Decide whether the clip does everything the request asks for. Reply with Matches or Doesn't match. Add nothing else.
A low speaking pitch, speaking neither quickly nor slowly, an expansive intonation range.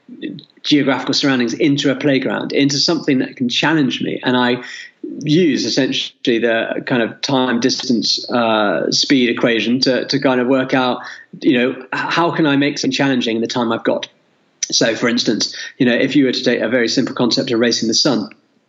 Doesn't match